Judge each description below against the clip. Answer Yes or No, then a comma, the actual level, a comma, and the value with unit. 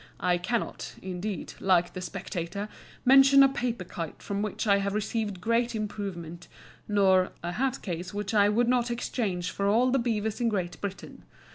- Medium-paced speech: Yes, average, 170 wpm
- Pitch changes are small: No, average, 4.2 semitones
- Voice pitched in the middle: No, high, 205 Hz